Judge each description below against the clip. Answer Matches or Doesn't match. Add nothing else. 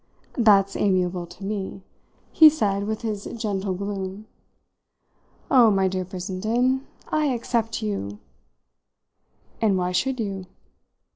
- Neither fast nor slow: Doesn't match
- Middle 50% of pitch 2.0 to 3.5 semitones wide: Matches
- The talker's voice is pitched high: Matches